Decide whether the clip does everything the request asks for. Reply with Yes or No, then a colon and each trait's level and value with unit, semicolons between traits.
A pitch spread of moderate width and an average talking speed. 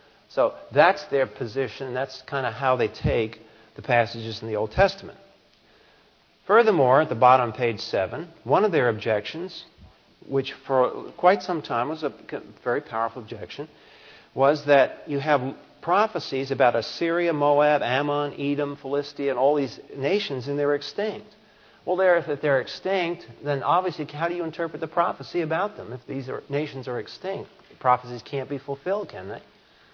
Yes: average, 4.4 semitones; average, 165 wpm